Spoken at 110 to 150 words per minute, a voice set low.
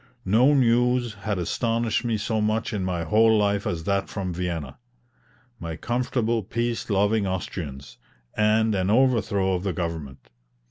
Yes: average, 145 wpm; low, 105 Hz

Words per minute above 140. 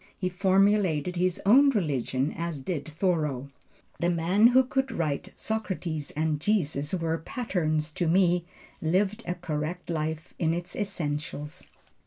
No: slow, 135 wpm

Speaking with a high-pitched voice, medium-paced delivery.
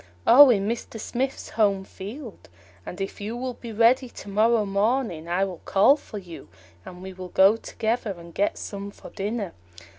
Yes: high, 205 Hz; average, 180 wpm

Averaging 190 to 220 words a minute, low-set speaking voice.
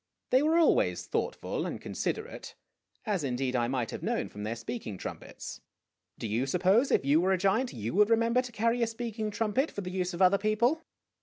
No: fast, 205 wpm; high, 200 Hz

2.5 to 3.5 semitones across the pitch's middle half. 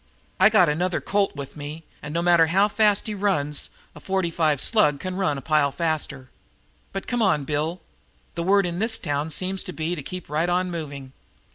No: average, 4.3 semitones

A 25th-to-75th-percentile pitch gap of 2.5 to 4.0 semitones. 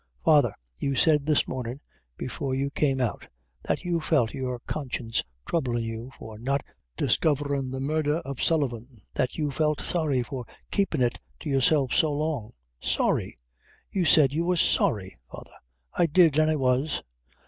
Yes: average, 3.5 semitones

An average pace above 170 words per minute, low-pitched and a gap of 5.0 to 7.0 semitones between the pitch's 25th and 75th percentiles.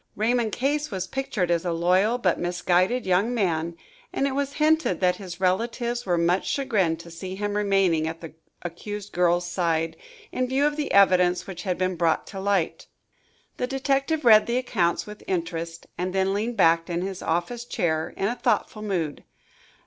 No: average, 180 wpm; high, 190 Hz; average, 5.3 semitones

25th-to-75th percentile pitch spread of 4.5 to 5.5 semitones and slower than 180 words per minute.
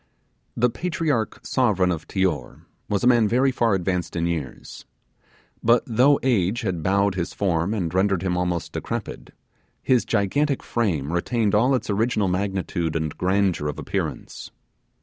Yes: average, 4.9 semitones; average, 145 wpm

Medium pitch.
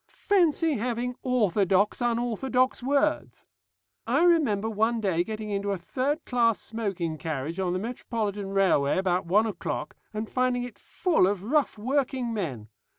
No: high, 220 Hz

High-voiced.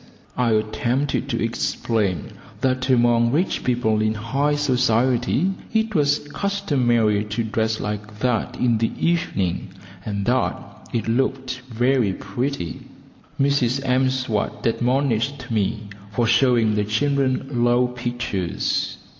No: low, 120 Hz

